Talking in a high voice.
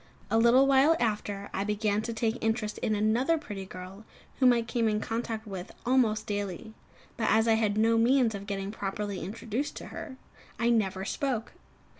Yes: high, 220 Hz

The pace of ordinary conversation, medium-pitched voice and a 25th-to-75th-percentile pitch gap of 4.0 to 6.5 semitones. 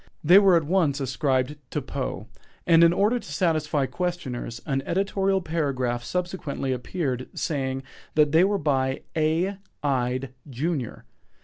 No: slow, 130 wpm; medium, 150 Hz; average, 4.9 semitones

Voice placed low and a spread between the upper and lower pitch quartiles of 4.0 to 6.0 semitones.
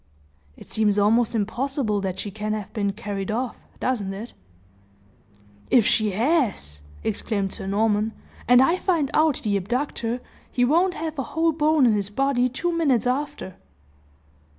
No: high, 230 Hz; average, 5.3 semitones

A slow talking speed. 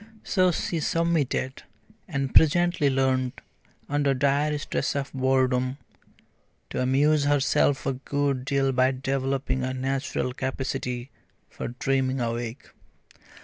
Yes: slow, 110 wpm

